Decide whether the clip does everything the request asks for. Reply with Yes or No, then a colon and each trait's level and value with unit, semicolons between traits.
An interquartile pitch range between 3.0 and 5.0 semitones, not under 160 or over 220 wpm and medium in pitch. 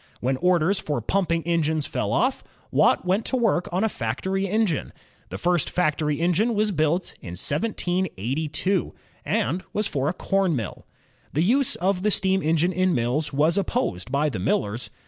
Yes: average, 4.6 semitones; average, 165 wpm; medium, 170 Hz